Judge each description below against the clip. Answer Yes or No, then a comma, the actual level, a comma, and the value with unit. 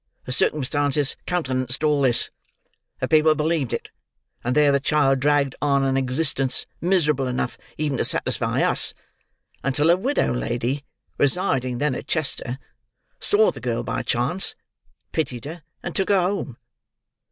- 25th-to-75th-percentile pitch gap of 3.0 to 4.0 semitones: Yes, average, 3.3 semitones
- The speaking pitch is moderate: Yes, medium, 145 Hz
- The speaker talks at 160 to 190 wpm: No, average, 145 wpm